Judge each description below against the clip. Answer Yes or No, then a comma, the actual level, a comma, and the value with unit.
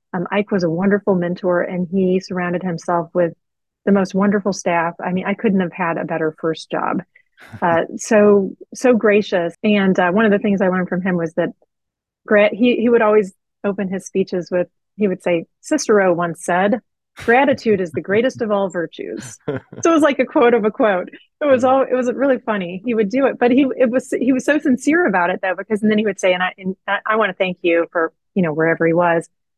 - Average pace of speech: No, fast, 230 wpm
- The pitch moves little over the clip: No, average, 4.1 semitones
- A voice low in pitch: No, high, 195 Hz